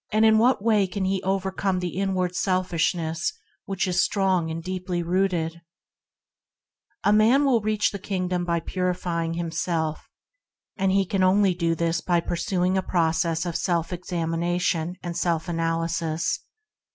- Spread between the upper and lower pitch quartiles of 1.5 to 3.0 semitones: Yes, narrow, 2.4 semitones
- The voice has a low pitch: No, medium, 180 Hz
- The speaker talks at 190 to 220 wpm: No, average, 145 wpm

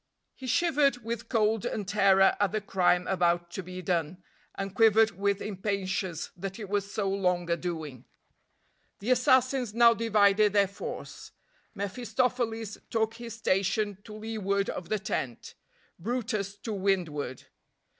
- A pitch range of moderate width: Yes, average, 3.2 semitones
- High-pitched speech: Yes, high, 200 Hz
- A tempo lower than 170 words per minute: Yes, average, 140 wpm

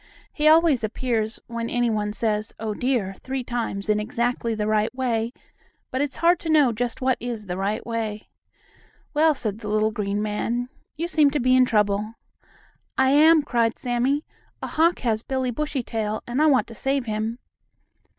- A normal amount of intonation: Yes, average, 3.7 semitones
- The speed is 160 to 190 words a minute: Yes, average, 180 wpm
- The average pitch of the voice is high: Yes, high, 235 Hz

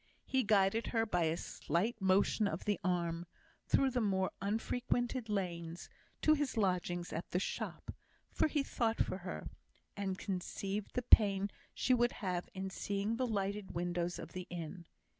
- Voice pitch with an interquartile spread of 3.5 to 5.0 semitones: Yes, average, 4.0 semitones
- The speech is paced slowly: No, average, 160 wpm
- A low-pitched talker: No, high, 195 Hz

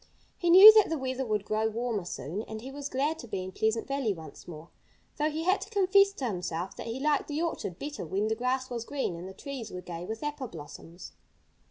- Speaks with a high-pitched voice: Yes, high, 240 Hz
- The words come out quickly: Yes, fast, 235 wpm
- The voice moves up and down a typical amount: No, wide, 7.4 semitones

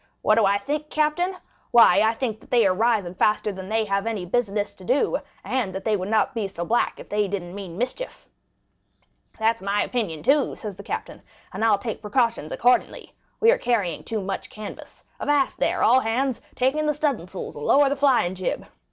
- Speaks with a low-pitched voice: No, high, 220 Hz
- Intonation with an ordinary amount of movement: Yes, average, 4.7 semitones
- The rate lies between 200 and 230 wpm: Yes, fast, 205 wpm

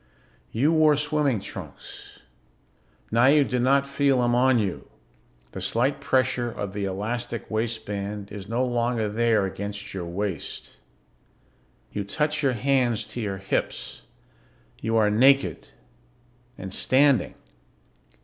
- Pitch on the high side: No, low, 120 Hz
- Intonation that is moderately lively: Yes, average, 4.5 semitones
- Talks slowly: Yes, slow, 125 wpm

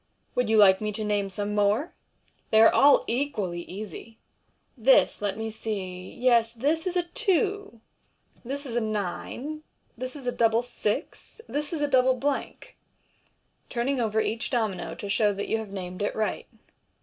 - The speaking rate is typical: Yes, average, 180 wpm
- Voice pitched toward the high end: Yes, high, 225 Hz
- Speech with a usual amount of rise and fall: Yes, average, 4.4 semitones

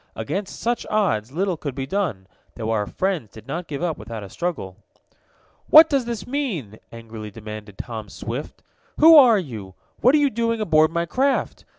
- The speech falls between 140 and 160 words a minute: No, average, 180 wpm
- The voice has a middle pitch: Yes, medium, 155 Hz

